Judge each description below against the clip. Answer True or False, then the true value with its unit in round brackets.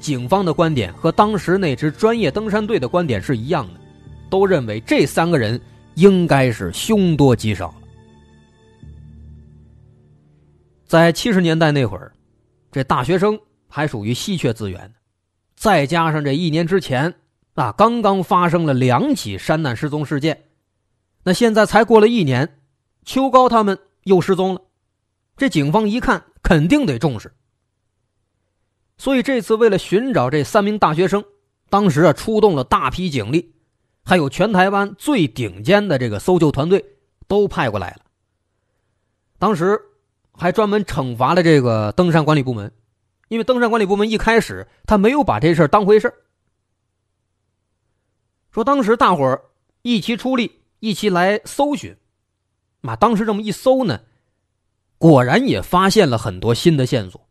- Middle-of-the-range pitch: True (155 Hz)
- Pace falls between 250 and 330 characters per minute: False (230 characters per minute)